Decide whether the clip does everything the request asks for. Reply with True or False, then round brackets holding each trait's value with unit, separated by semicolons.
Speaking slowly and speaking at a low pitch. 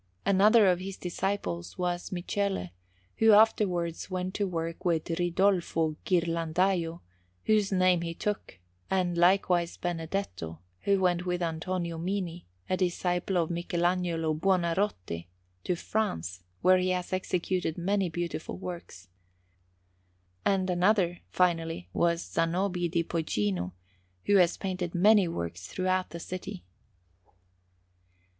False (115 wpm; 175 Hz)